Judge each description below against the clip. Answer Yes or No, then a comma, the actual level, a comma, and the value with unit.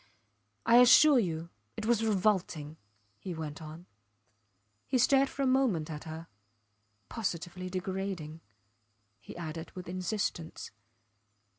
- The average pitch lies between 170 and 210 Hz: Yes, medium, 185 Hz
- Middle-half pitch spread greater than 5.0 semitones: Yes, wide, 5.6 semitones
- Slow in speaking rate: Yes, slow, 115 wpm